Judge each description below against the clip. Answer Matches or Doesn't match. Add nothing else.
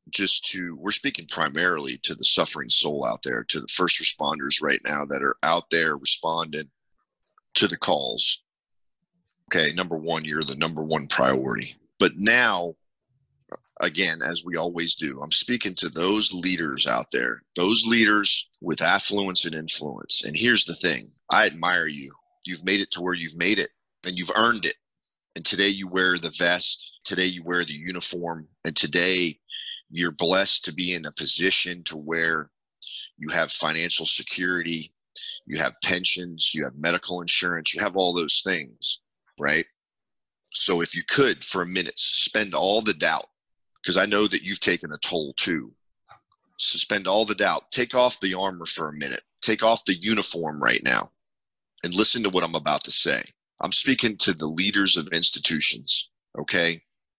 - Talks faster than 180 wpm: Doesn't match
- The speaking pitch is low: Matches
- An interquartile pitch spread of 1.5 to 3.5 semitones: Matches